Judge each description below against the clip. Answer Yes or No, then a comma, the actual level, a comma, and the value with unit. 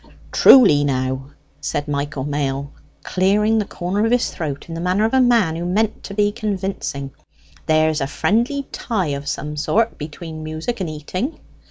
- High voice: No, medium, 170 Hz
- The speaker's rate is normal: Yes, average, 170 wpm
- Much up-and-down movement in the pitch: Yes, wide, 6.5 semitones